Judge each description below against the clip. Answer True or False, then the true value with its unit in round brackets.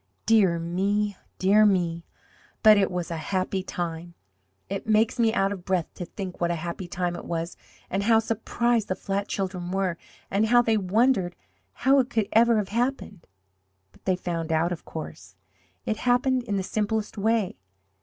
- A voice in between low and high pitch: False (195 Hz)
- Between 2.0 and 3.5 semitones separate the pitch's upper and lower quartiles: False (3.9 semitones)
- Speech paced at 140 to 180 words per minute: True (175 wpm)